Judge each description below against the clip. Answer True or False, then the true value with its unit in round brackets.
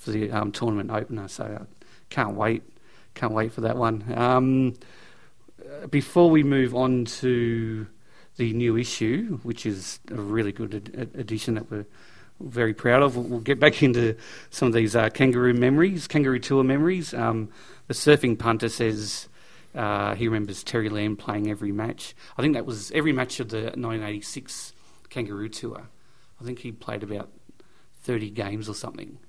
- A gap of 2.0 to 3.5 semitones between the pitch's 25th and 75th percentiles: True (2.7 semitones)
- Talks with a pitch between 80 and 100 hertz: False (115 Hz)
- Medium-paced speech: True (170 wpm)